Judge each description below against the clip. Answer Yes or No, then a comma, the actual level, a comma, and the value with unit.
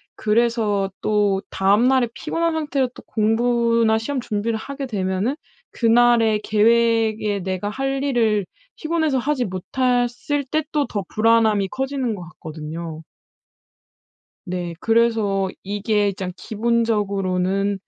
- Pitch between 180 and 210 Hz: No, high, 225 Hz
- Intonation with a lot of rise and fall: No, average, 3.5 semitones